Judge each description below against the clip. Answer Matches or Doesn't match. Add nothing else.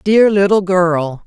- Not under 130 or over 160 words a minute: Matches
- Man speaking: Doesn't match